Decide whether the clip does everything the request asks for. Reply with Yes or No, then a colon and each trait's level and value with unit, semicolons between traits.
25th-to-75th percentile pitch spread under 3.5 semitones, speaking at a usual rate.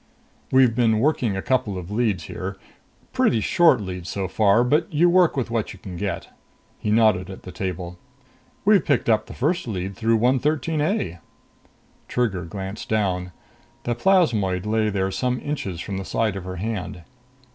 No: average, 4.9 semitones; average, 170 wpm